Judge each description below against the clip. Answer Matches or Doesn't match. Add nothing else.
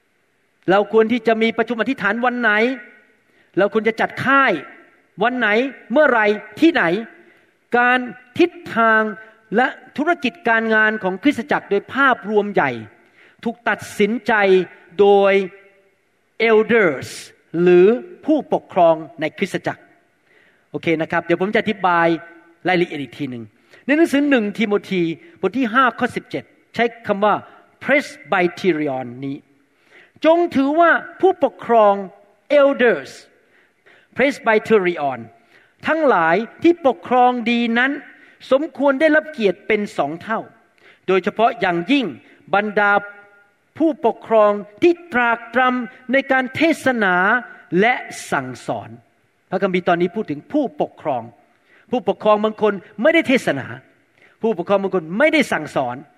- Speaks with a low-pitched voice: Doesn't match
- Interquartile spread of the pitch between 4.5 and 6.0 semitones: Matches